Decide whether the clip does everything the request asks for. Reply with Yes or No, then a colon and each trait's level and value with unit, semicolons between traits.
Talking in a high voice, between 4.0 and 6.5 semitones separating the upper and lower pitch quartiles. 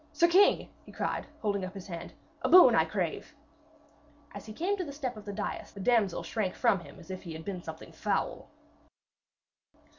Yes: high, 205 Hz; average, 5.2 semitones